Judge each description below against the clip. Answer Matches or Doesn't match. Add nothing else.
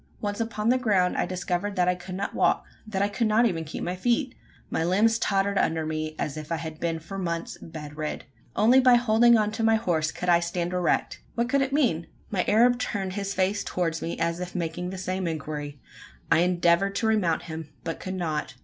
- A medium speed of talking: Doesn't match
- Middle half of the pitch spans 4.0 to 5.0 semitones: Matches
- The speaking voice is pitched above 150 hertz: Matches